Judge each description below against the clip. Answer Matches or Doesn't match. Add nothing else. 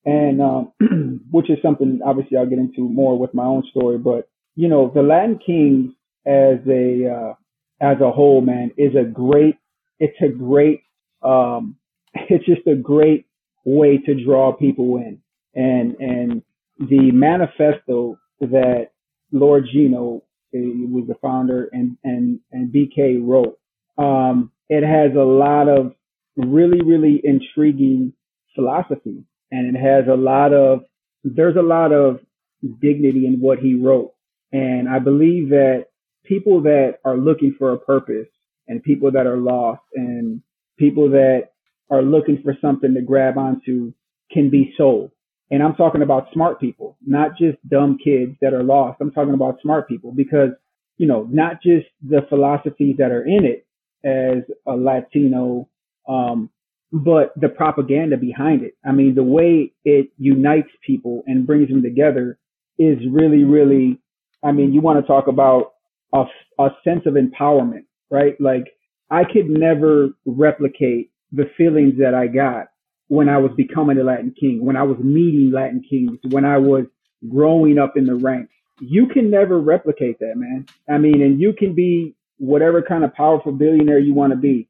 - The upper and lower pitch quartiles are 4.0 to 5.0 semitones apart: Doesn't match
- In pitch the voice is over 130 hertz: Matches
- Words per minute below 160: Doesn't match